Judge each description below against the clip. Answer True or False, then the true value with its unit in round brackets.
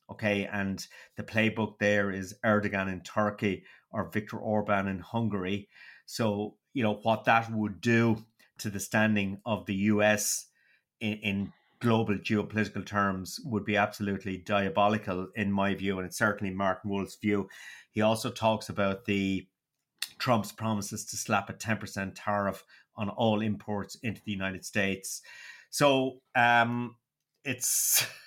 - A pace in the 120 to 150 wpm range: True (140 wpm)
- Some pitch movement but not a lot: False (1.9 semitones)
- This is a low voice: True (105 Hz)